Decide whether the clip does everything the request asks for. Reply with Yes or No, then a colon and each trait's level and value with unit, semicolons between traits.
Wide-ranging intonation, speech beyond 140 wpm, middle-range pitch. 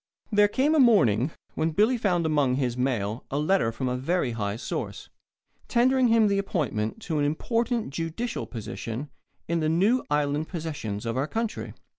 Yes: wide, 8.7 semitones; average, 170 wpm; medium, 155 Hz